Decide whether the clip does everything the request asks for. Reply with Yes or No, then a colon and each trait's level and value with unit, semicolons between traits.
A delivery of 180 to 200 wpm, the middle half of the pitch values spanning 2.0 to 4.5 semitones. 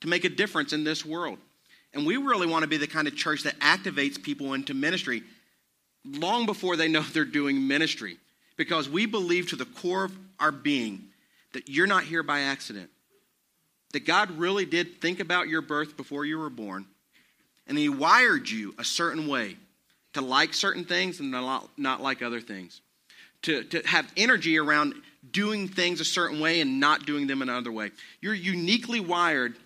No: average, 185 wpm; average, 5.1 semitones